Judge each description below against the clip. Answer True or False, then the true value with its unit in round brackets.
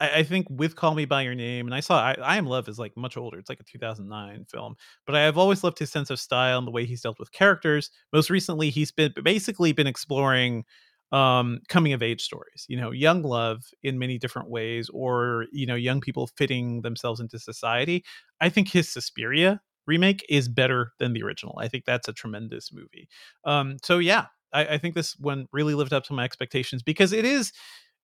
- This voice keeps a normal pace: False (215 wpm)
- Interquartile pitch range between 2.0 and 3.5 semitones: False (4.6 semitones)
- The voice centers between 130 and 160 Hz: True (135 Hz)